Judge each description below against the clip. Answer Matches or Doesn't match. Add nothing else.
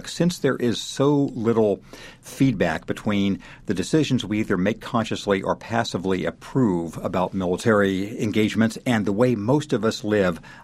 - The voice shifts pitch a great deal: Doesn't match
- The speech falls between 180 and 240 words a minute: Doesn't match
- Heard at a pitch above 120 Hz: Doesn't match